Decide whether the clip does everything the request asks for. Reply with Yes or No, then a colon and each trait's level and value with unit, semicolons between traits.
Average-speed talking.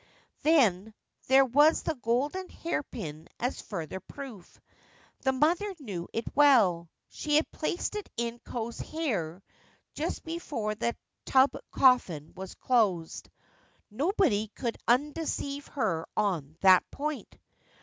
No: slow, 120 wpm